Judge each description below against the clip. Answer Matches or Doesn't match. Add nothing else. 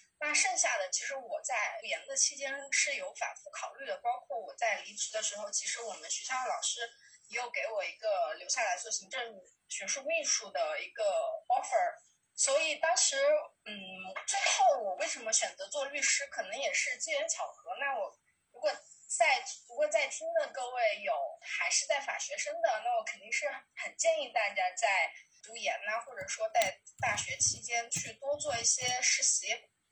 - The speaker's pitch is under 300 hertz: Doesn't match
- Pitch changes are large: Doesn't match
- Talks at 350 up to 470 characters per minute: Doesn't match